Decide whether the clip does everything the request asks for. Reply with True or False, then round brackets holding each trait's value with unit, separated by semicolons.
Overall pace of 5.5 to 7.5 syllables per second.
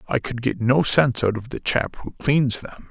False (5.0 syllables/s)